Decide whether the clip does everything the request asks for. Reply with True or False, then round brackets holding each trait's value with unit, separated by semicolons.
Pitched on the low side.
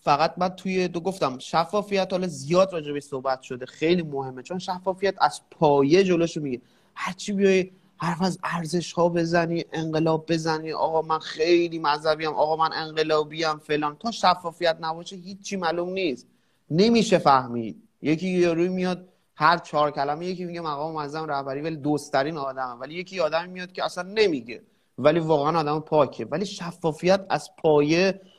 False (165 Hz)